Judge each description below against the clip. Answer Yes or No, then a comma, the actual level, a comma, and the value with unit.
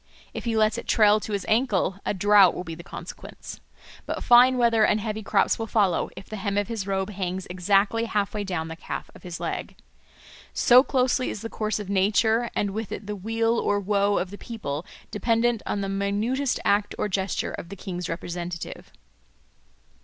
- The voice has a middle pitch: No, high, 205 Hz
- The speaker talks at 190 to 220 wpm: Yes, average, 200 wpm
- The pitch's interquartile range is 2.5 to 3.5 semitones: Yes, average, 2.8 semitones